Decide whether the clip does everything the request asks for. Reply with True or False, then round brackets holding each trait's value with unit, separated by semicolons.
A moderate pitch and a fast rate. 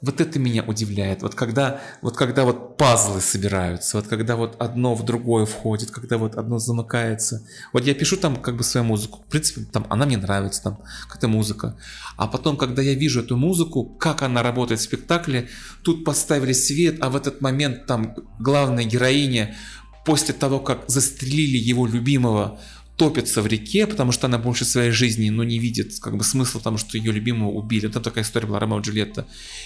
False (120 Hz; 195 wpm)